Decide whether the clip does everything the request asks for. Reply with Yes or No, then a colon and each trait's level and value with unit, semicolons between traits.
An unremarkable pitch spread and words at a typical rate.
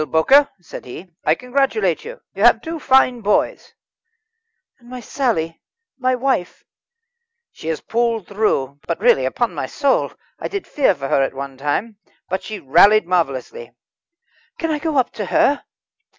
No: wide, 8.7 semitones; average, 165 wpm